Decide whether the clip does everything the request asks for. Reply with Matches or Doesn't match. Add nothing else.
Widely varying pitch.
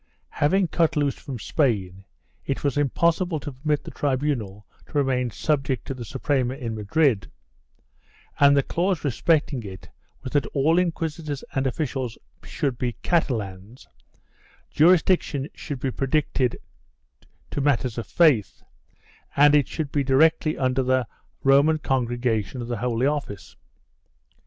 Doesn't match